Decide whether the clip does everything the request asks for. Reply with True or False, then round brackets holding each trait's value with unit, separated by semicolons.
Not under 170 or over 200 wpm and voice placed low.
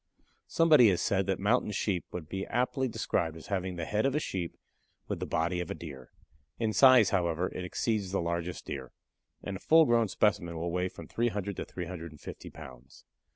True (195 wpm; 95 Hz)